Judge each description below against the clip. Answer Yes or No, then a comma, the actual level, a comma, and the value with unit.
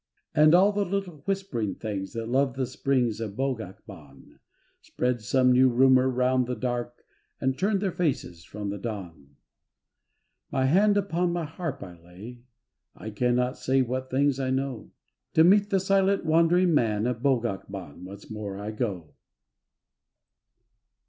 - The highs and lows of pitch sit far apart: Yes, wide, 6.8 semitones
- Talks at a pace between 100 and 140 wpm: No, average, 155 wpm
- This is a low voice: Yes, low, 125 Hz